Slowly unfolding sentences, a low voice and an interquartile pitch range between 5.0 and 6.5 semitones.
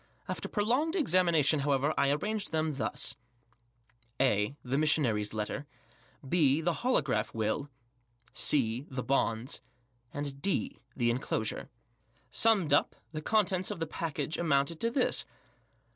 No: slow, 120 wpm; medium, 145 Hz; average, 5.3 semitones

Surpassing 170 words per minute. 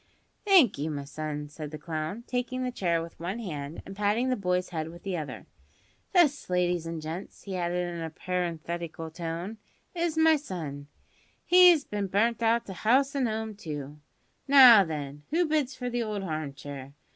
Yes: average, 180 wpm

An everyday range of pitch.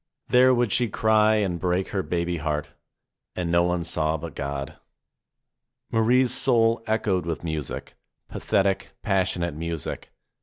Yes: average, 4.8 semitones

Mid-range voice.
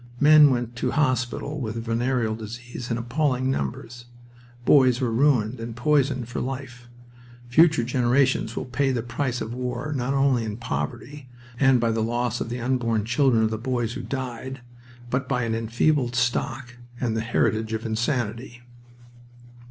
No: low, 120 Hz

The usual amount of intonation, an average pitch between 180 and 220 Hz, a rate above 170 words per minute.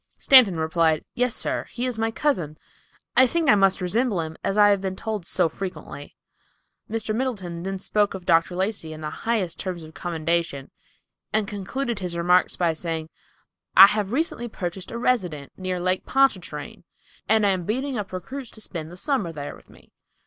Yes: average, 4.8 semitones; high, 190 Hz; average, 180 wpm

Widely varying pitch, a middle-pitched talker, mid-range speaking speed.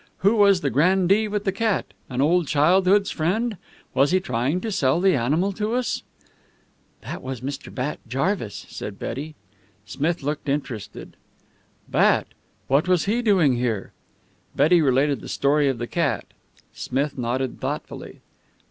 Yes: wide, 6.3 semitones; medium, 150 Hz; average, 150 wpm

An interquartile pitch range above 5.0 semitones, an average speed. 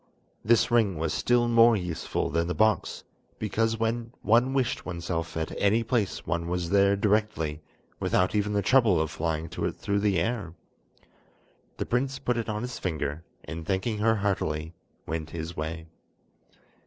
Yes: wide, 5.6 semitones; average, 165 wpm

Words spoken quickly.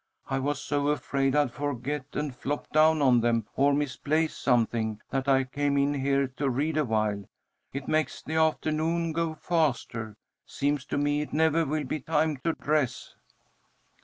No: average, 160 wpm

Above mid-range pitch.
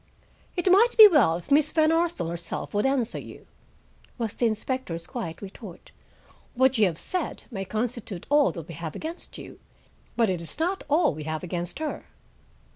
Yes: high, 235 Hz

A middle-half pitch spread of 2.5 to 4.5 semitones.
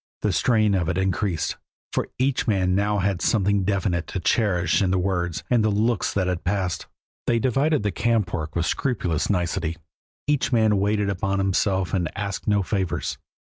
Yes: average, 2.8 semitones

